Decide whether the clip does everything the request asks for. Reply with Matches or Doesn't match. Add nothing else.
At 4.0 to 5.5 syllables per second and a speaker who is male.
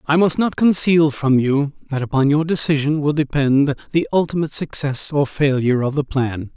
Matches